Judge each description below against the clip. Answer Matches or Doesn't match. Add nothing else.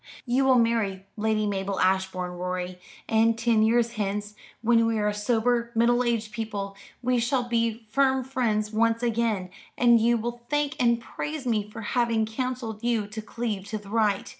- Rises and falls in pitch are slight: Matches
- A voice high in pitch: Matches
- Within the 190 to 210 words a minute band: Doesn't match